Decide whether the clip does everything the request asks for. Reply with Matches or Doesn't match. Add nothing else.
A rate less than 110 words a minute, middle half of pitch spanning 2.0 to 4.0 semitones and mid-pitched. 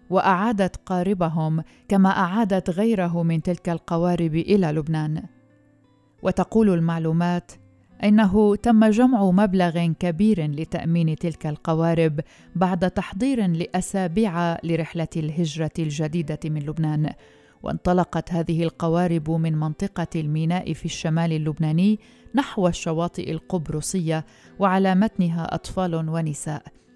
Matches